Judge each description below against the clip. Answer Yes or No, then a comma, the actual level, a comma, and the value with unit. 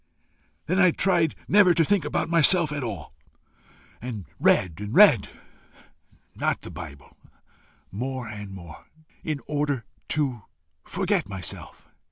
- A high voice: No, medium, 140 Hz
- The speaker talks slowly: Yes, slow, 125 wpm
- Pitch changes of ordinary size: No, wide, 8.2 semitones